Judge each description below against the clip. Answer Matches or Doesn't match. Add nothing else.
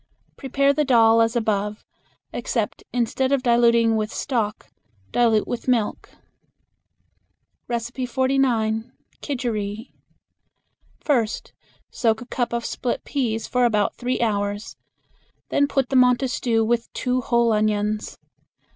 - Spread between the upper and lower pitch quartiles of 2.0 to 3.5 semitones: Matches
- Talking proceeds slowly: Matches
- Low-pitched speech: Doesn't match